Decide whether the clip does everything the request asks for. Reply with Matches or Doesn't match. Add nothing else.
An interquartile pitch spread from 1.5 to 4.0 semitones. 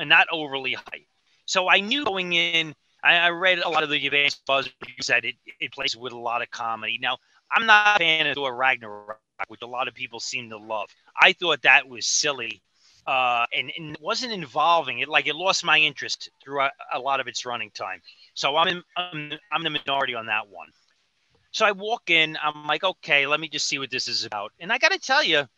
Doesn't match